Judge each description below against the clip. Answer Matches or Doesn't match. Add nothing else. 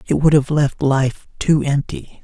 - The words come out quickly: Doesn't match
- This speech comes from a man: Matches